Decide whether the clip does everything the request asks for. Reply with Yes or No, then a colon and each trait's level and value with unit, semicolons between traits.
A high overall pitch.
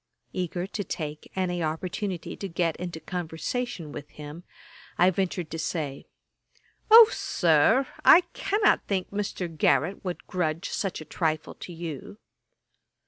No: medium, 175 Hz